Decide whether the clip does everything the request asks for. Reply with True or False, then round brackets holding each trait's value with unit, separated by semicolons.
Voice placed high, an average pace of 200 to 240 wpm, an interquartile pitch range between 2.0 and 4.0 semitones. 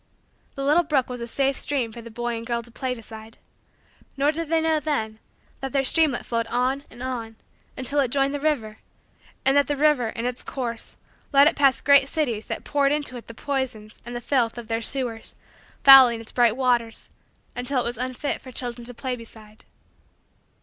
True (250 Hz; 205 wpm; 3.2 semitones)